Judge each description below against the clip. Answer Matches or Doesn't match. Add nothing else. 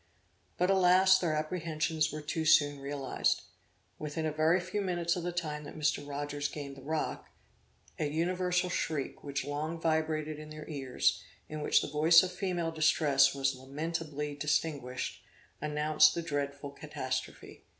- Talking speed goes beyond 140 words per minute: Matches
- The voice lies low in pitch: Doesn't match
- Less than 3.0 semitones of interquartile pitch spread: Matches